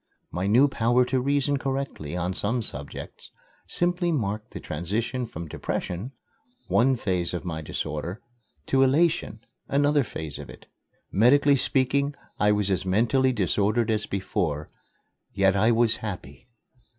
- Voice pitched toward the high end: No, low, 110 Hz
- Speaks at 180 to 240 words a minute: No, average, 140 wpm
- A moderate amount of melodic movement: No, wide, 6.2 semitones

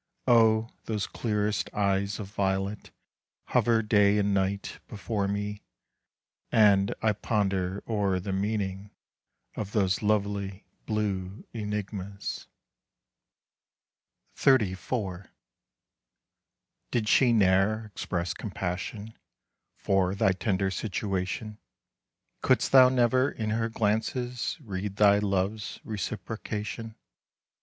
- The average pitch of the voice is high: No, low, 105 Hz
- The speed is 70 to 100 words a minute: Yes, slow, 95 wpm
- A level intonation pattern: Yes, narrow, 2.1 semitones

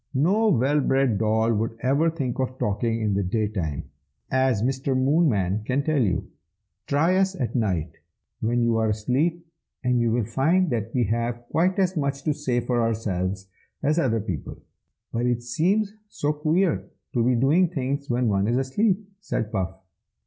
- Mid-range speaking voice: No, low, 125 Hz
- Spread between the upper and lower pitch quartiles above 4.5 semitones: Yes, average, 5.1 semitones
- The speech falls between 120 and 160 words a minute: No, average, 175 wpm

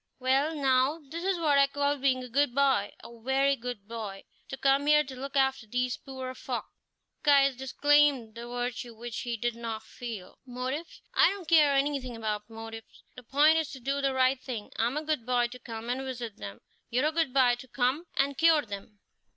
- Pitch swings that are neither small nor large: Yes, average, 3.0 semitones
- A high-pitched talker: Yes, very high, 260 Hz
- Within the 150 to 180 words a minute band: No, fast, 205 wpm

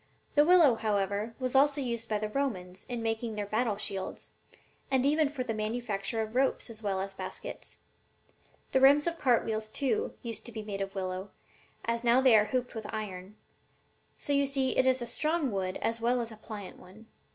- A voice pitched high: Yes, high, 230 Hz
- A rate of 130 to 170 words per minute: No, average, 200 wpm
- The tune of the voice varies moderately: Yes, average, 3.9 semitones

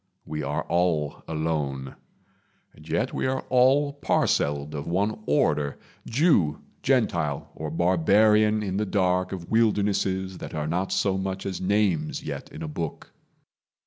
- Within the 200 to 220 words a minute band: No, average, 145 wpm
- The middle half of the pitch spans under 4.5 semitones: No, wide, 5.4 semitones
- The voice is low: Yes, very low, 90 Hz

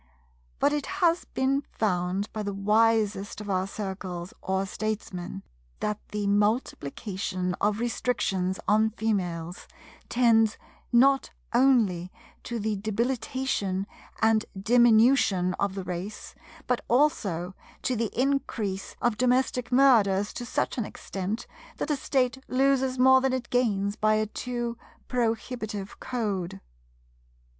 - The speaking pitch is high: Yes, high, 215 Hz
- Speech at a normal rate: No, slow, 120 wpm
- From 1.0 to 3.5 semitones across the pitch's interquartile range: No, average, 4.2 semitones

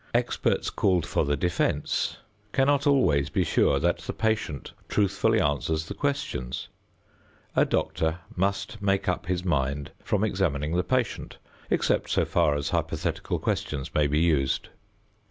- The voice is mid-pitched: No, very low, 85 Hz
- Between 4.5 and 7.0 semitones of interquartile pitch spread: Yes, wide, 5.6 semitones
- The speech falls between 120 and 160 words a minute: Yes, average, 140 wpm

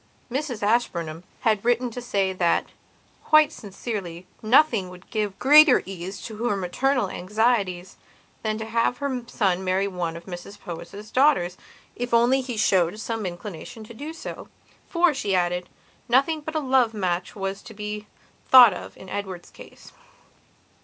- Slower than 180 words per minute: Yes, average, 160 wpm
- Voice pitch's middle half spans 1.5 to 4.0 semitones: No, average, 4.9 semitones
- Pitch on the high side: Yes, high, 210 Hz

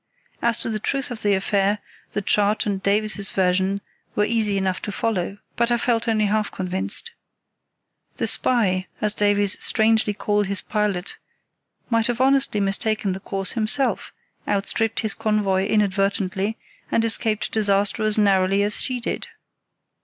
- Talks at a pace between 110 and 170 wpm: Yes, average, 150 wpm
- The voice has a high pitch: Yes, high, 210 Hz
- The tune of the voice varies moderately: No, narrow, 2.1 semitones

